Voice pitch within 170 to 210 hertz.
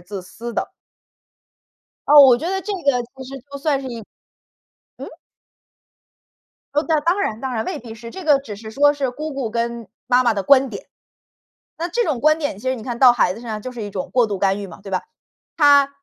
No: very high, 255 Hz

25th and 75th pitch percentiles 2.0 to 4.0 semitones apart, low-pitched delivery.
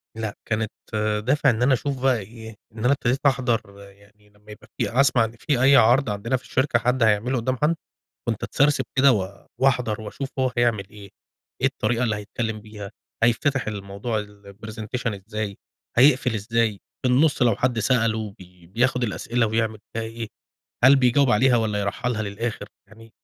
Yes: average, 3.2 semitones; low, 115 Hz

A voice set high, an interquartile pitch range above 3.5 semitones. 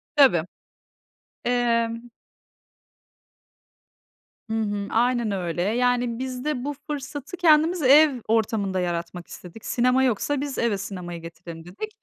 Yes: high, 235 Hz; average, 5.2 semitones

